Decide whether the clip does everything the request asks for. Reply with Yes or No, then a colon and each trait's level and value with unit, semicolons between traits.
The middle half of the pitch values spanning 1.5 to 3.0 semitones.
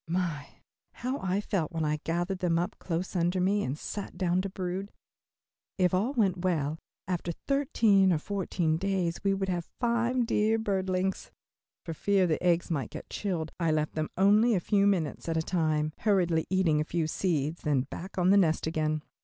No: average, 3.4 semitones